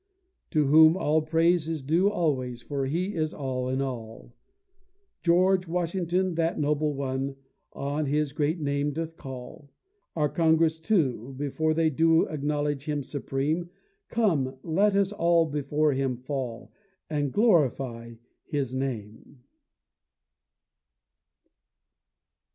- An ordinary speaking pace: No, slow, 115 wpm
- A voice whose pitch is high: No, medium, 150 Hz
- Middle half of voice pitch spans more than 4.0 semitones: No, average, 3.4 semitones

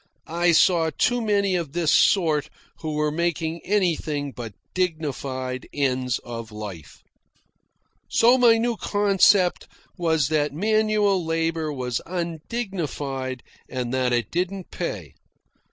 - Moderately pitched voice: Yes, medium, 160 Hz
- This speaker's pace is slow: Yes, slow, 120 wpm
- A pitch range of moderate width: No, wide, 5.8 semitones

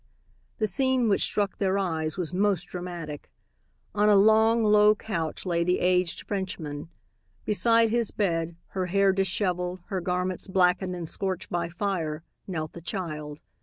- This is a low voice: No, medium, 185 Hz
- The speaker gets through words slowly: No, average, 150 wpm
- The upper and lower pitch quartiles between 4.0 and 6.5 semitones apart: No, average, 3.0 semitones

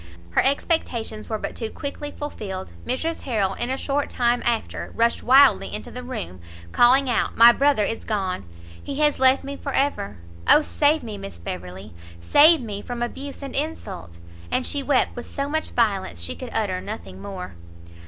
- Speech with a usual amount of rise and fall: No, wide, 6.3 semitones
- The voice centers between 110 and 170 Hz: No, high, 240 Hz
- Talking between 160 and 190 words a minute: Yes, average, 180 wpm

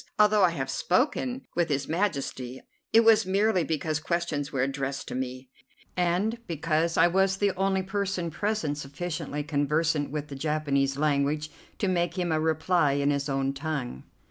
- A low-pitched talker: No, medium, 155 Hz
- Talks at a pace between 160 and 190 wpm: Yes, average, 165 wpm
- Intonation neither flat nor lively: Yes, average, 4.6 semitones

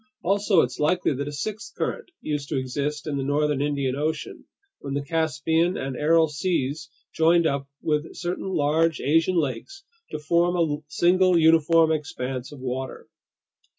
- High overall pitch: No, medium, 155 Hz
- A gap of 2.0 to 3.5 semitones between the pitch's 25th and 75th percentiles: Yes, average, 2.9 semitones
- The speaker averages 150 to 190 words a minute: Yes, average, 155 wpm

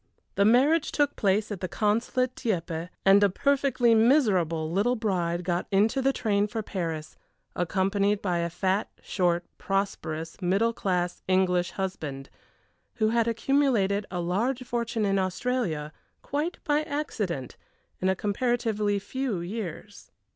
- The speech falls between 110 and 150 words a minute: Yes, average, 140 wpm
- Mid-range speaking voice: No, high, 200 Hz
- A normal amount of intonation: Yes, average, 4.8 semitones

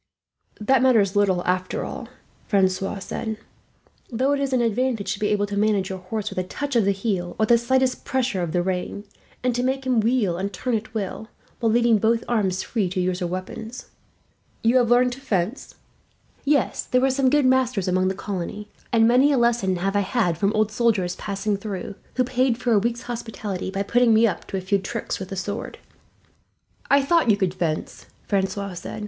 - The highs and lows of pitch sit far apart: No, average, 4.2 semitones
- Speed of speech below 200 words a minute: No, fast, 205 wpm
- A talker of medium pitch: No, high, 215 Hz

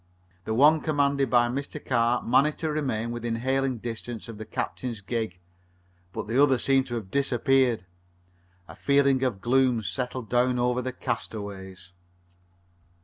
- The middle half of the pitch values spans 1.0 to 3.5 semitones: Yes, average, 2.9 semitones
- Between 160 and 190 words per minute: No, average, 145 wpm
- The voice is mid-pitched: No, low, 125 Hz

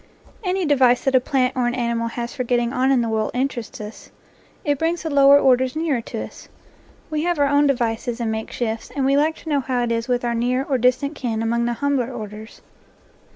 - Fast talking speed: Yes, fast, 240 wpm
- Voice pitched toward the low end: No, very high, 250 Hz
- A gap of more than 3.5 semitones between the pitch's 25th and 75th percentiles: No, average, 3.0 semitones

